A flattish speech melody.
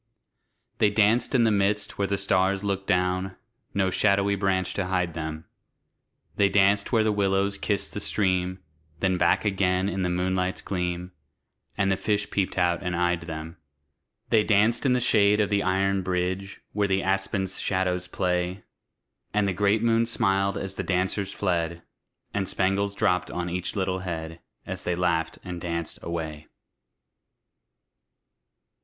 Yes: narrow, 2.0 semitones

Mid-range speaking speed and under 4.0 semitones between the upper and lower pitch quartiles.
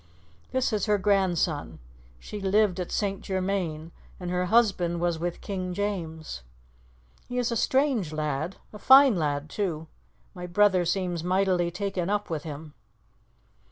Yes: average, 145 wpm; average, 3.3 semitones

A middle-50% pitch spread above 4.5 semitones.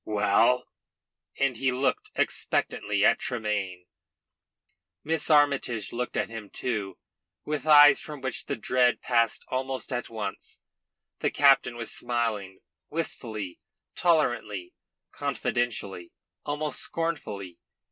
Yes: average, 4.9 semitones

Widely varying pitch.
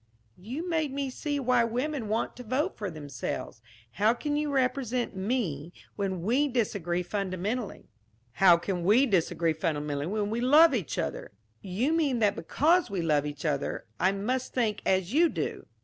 Yes: wide, 6.6 semitones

